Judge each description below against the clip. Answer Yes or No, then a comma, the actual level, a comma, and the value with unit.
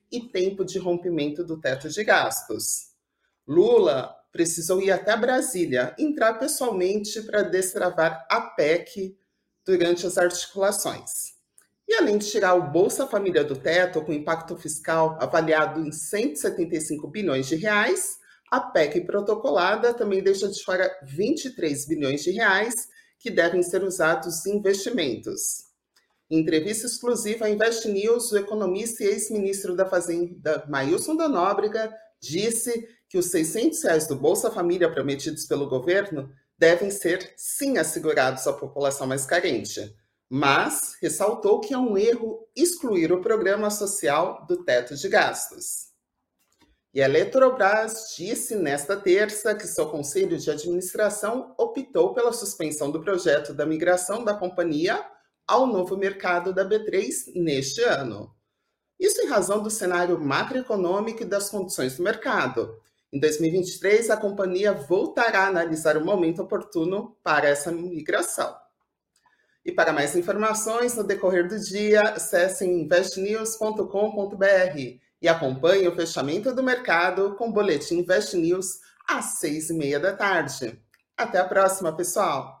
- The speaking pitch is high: Yes, high, 195 Hz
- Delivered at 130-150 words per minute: Yes, average, 135 wpm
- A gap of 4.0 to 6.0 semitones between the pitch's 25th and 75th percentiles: Yes, average, 5.0 semitones